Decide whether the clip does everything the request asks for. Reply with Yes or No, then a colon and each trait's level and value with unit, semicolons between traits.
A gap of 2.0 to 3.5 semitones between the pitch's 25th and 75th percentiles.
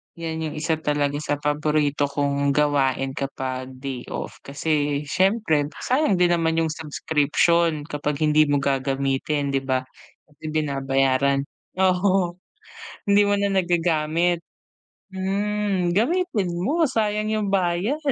No: average, 4.7 semitones